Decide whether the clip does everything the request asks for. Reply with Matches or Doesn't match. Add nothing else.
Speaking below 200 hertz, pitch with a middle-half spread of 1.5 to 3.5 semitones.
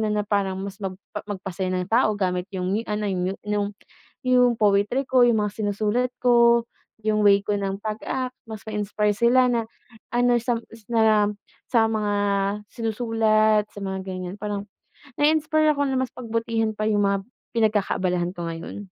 Doesn't match